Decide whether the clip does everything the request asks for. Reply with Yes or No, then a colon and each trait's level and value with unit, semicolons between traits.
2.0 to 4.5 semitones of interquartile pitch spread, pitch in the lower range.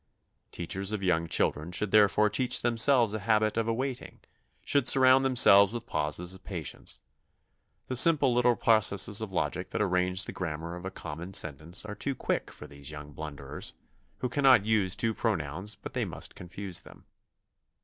No: average, 5.1 semitones; low, 100 Hz